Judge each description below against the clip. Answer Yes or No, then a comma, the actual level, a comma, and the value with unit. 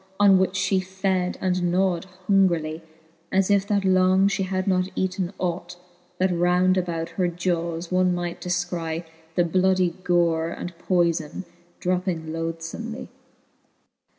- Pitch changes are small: Yes, narrow, 1.6 semitones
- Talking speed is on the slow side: Yes, slow, 130 wpm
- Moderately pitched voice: Yes, medium, 180 Hz